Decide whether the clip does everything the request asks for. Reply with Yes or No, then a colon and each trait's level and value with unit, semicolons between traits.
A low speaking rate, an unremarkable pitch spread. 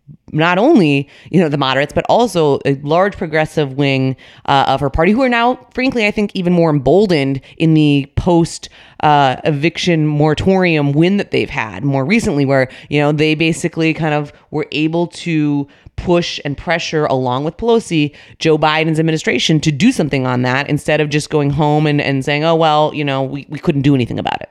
No: average, 195 wpm; average, 3.1 semitones